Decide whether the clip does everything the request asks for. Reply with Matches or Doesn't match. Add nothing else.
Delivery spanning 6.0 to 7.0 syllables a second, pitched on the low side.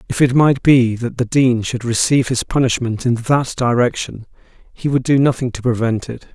Doesn't match